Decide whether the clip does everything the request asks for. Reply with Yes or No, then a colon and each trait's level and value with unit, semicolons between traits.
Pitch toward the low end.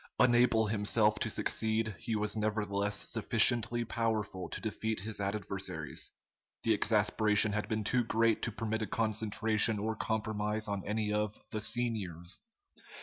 Yes: low, 110 Hz